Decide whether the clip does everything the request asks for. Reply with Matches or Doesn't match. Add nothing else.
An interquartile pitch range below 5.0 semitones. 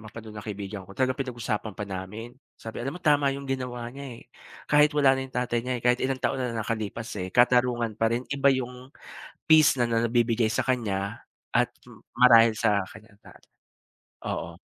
Matches